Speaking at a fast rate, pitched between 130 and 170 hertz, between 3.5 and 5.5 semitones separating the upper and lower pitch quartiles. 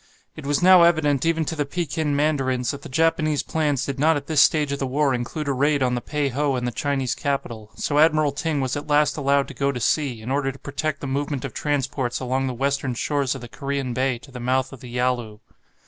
No: fast, 245 wpm; medium, 140 Hz; narrow, 2.4 semitones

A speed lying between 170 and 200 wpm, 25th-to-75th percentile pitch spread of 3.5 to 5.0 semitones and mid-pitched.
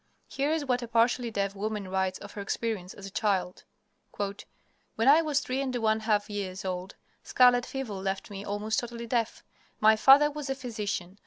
No: average, 185 wpm; average, 3.9 semitones; high, 220 Hz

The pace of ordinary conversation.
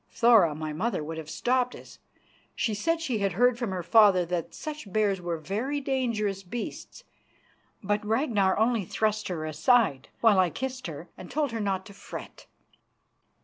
Yes: average, 170 wpm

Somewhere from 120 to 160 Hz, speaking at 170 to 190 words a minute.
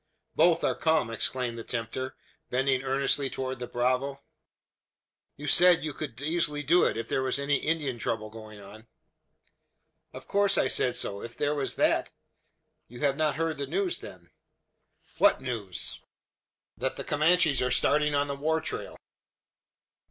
No: low, 135 Hz; average, 160 wpm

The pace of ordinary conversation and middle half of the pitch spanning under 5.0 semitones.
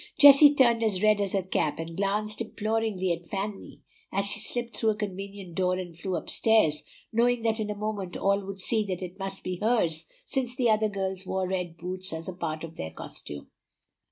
No: fast, 210 wpm; average, 3.1 semitones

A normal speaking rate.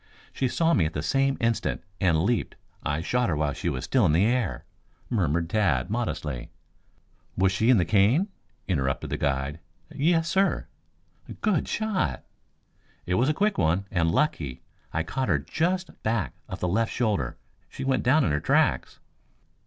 Yes: average, 170 wpm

